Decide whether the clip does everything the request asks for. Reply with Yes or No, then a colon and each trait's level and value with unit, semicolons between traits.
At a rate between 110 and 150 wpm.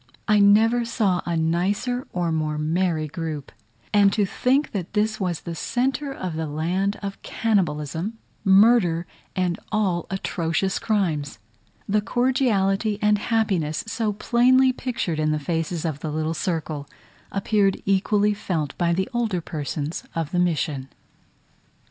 Yes: average, 140 wpm